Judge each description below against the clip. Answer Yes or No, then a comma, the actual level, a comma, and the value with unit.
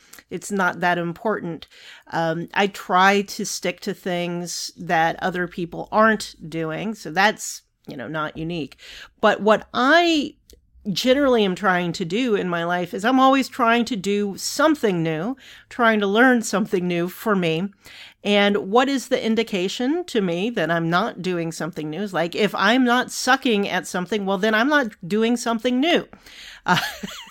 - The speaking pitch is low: No, high, 205 Hz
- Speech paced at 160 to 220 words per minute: Yes, average, 170 wpm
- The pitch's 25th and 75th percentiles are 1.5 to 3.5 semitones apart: No, average, 4.8 semitones